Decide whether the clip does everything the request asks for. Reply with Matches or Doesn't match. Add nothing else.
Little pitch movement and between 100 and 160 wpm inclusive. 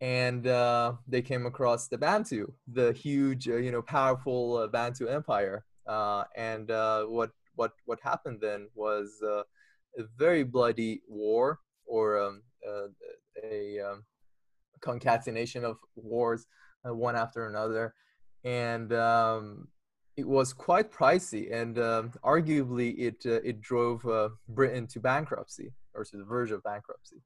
Matches